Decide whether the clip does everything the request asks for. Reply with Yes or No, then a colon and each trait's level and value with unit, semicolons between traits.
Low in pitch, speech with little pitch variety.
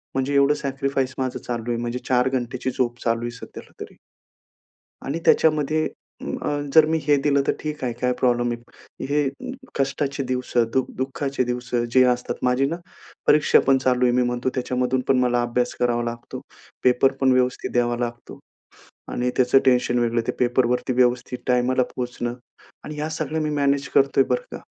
Yes: low, 125 Hz; narrow, 2.0 semitones